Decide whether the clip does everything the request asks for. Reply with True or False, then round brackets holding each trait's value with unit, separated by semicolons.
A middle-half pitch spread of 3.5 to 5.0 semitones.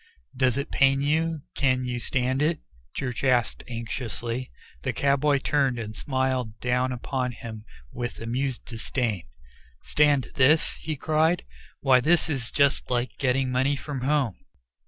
False (2.5 semitones)